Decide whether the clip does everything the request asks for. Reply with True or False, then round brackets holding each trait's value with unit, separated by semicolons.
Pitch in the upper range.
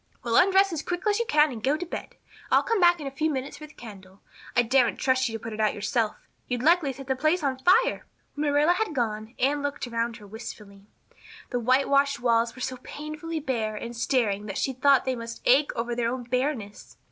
True (260 Hz)